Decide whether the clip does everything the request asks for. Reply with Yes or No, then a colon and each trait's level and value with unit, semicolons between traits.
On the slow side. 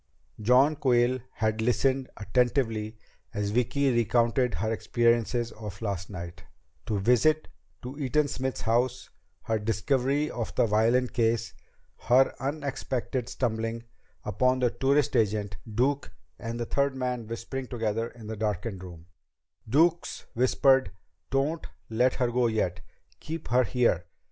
Yes: slow, 130 wpm